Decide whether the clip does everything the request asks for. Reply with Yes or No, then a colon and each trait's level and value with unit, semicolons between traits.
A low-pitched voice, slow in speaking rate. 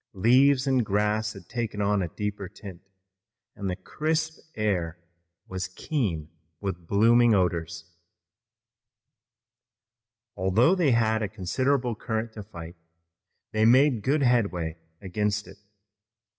Yes: low, 105 Hz; slow, 120 wpm